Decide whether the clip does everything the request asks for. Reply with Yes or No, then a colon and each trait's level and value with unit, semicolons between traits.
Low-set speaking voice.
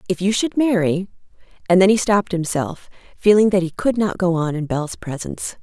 No: high, 190 Hz